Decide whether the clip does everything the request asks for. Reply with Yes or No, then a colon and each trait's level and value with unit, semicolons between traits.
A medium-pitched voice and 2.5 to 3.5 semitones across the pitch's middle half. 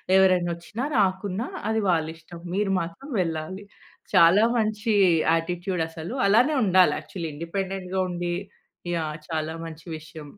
Yes: medium, 180 Hz; average, 3.2 semitones